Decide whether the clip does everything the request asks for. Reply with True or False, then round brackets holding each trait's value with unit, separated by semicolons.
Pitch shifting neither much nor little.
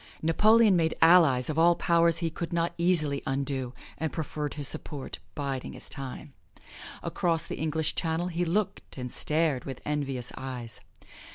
True (3.7 semitones)